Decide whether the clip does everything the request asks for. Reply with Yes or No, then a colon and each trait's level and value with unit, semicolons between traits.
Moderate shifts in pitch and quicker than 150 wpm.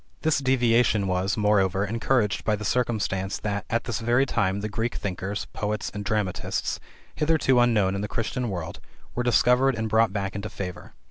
Yes: average, 3.5 semitones; average, 175 wpm